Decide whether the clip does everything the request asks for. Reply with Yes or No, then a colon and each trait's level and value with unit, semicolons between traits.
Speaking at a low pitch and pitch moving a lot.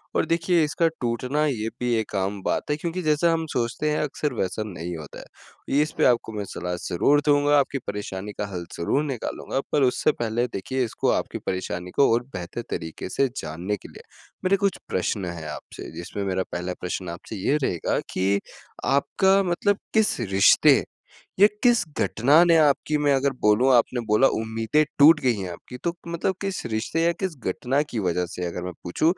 Yes: low, 120 Hz; wide, 8.0 semitones